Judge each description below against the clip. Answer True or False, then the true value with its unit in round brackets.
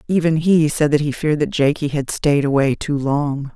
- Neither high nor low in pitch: True (150 Hz)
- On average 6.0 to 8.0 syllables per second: False (5.0 syllables/s)